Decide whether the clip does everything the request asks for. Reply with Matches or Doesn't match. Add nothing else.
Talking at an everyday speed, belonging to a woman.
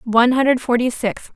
Matches